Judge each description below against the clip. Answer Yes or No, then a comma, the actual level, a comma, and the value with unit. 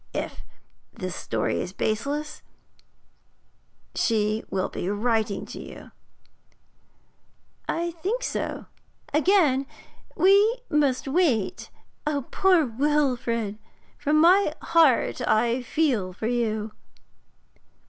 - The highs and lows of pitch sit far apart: Yes, wide, 6.7 semitones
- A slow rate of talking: Yes, slow, 90 wpm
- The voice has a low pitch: No, very high, 260 Hz